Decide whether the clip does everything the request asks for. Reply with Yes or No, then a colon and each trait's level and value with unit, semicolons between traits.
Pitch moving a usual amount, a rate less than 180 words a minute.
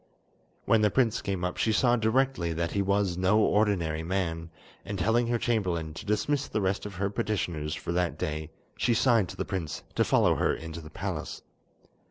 No: average, 4.5 semitones; average, 195 wpm